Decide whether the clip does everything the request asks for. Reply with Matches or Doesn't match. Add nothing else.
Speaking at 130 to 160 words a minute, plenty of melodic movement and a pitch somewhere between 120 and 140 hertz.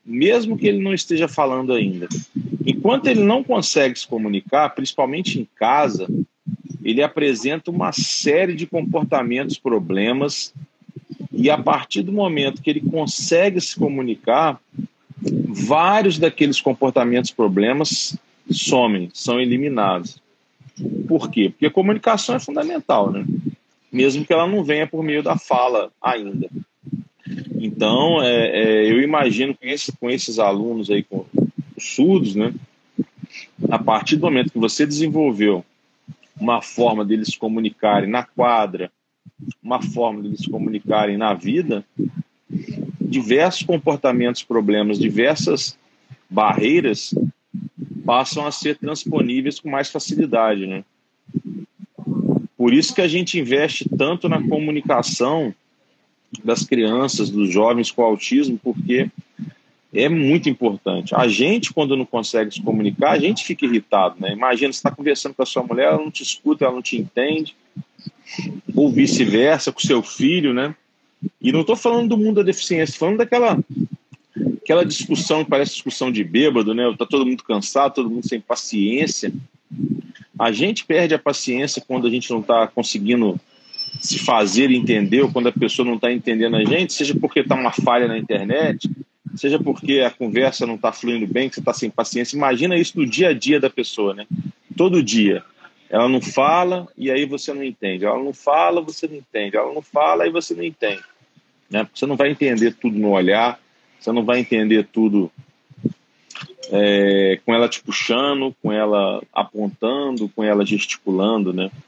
Matches